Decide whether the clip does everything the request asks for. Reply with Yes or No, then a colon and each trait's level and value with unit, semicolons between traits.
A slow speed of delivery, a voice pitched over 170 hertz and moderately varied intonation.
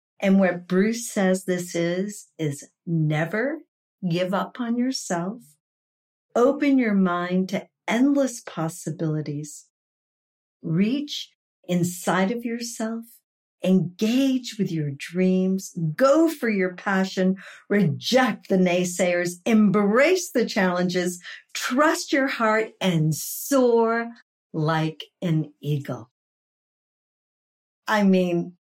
Yes: slow, 95 wpm; high, 190 Hz; average, 4.9 semitones